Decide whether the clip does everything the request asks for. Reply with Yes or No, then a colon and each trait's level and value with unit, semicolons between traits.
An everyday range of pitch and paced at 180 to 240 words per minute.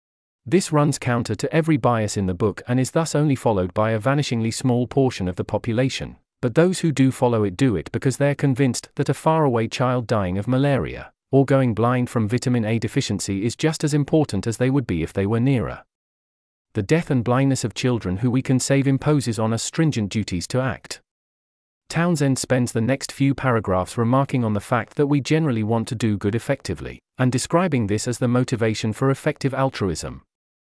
Yes: average, 3.8 semitones; average, 200 wpm